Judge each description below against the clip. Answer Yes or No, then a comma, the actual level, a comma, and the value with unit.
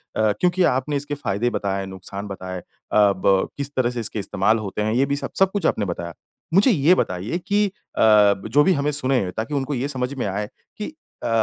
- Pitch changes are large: Yes, wide, 6.5 semitones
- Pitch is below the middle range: Yes, low, 125 Hz